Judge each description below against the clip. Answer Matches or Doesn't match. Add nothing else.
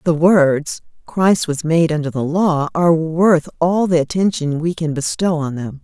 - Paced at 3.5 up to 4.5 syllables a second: Matches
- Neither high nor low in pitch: Matches